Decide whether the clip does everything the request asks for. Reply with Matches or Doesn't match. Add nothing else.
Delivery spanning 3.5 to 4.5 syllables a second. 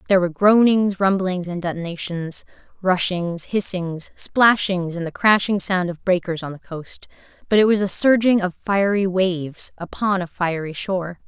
Doesn't match